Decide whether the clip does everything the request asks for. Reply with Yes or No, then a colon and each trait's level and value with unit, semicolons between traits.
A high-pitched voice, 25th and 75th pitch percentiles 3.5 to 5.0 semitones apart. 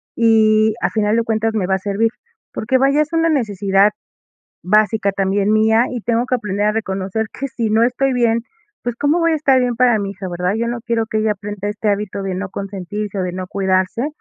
No: high, 215 Hz; average, 3.0 semitones